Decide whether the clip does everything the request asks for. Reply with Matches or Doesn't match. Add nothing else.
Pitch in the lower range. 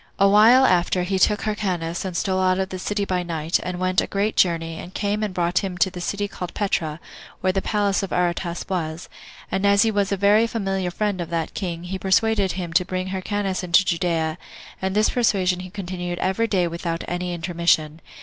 Doesn't match